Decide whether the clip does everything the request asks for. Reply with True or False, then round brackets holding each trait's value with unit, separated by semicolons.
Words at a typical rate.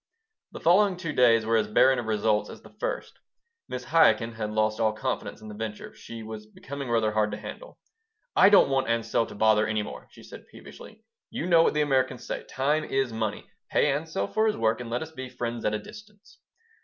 False (215 wpm)